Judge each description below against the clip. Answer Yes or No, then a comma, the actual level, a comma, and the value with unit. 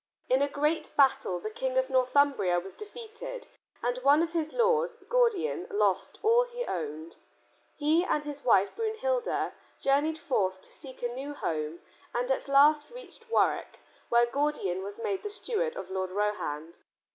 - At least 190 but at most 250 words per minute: No, average, 160 wpm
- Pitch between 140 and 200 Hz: No, very high, 285 Hz